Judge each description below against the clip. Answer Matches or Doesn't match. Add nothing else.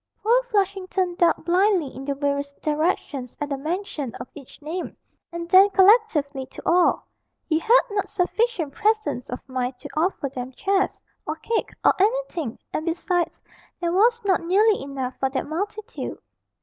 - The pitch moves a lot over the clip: Matches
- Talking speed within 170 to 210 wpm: Doesn't match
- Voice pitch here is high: Matches